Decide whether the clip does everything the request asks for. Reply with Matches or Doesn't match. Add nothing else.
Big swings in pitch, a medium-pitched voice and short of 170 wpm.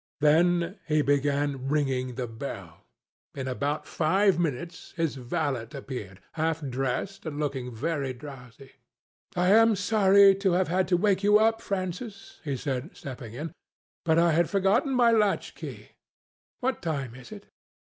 Matches